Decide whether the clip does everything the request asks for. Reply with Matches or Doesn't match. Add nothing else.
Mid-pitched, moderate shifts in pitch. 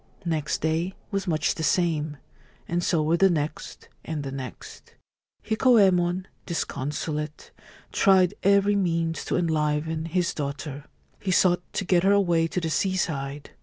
Matches